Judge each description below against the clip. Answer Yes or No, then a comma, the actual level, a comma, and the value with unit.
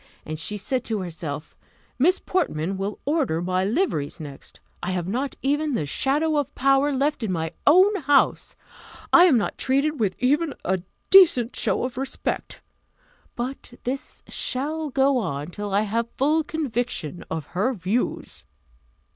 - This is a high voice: Yes, very high, 250 Hz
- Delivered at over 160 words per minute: No, average, 155 wpm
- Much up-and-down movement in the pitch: Yes, wide, 7.6 semitones